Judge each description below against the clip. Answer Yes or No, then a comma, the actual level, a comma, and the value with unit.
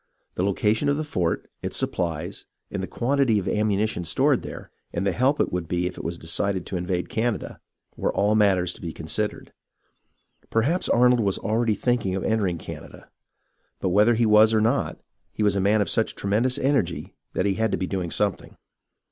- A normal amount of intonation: Yes, average, 3.7 semitones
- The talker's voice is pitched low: Yes, low, 105 Hz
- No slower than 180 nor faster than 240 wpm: Yes, average, 200 wpm